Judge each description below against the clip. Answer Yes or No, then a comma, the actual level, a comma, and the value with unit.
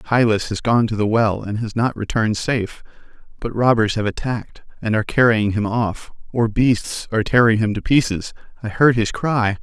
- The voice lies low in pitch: Yes, low, 110 Hz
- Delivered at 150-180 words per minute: No, average, 195 wpm